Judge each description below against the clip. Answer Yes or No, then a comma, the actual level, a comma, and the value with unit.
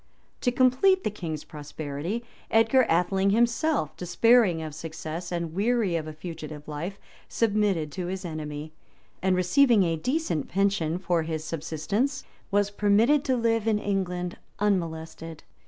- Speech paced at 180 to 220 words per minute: No, average, 140 wpm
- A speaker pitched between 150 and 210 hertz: Yes, medium, 185 Hz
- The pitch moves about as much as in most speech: No, wide, 5.7 semitones